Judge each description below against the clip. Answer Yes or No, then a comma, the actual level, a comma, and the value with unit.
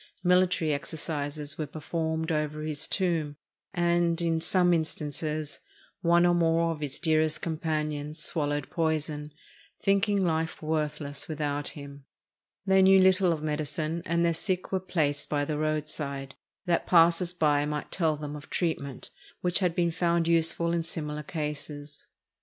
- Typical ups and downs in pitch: No, narrow, 2.3 semitones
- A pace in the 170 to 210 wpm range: No, average, 145 wpm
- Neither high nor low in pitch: Yes, medium, 160 Hz